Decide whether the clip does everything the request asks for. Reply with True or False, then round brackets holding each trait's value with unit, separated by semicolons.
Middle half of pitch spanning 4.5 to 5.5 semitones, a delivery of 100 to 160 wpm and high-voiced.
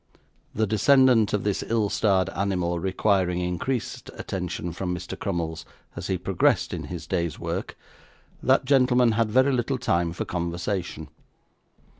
False (4.8 semitones; 140 wpm; 95 Hz)